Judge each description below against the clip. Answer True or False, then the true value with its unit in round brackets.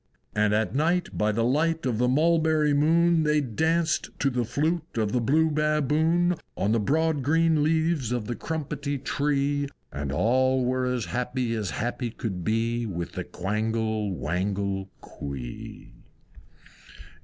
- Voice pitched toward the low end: True (130 Hz)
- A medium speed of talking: True (145 wpm)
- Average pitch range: False (6.0 semitones)